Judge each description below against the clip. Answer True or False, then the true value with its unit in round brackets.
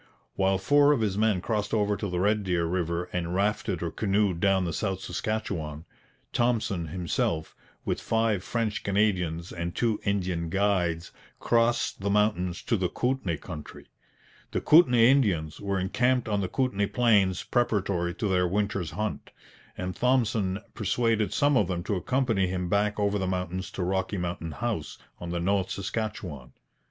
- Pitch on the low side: True (100 Hz)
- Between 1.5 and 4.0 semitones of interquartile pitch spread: True (3.5 semitones)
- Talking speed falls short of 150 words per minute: False (160 wpm)